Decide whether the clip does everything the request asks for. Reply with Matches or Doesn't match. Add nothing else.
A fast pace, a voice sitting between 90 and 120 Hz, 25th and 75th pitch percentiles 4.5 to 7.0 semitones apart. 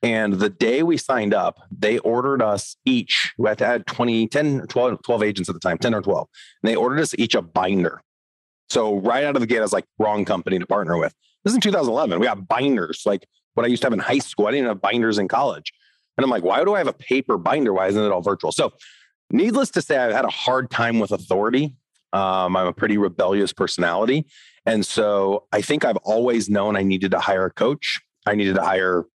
Matches